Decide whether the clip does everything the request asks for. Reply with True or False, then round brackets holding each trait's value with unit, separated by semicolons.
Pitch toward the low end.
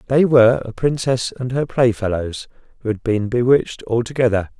True (120 Hz)